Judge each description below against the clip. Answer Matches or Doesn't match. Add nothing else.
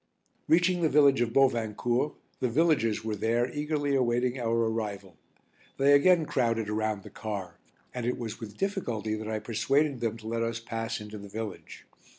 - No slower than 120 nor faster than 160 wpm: Doesn't match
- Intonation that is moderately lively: Matches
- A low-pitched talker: Matches